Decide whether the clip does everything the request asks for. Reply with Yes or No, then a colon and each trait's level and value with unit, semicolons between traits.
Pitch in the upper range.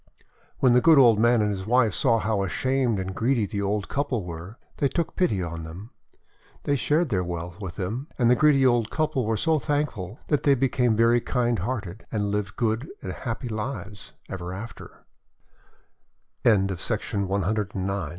No: low, 115 Hz